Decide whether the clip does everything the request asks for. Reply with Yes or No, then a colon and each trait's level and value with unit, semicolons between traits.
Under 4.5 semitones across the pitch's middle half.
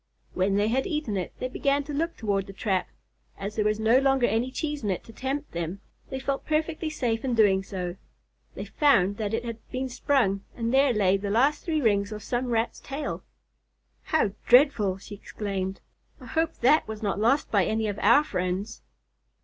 No: average, 5.3 semitones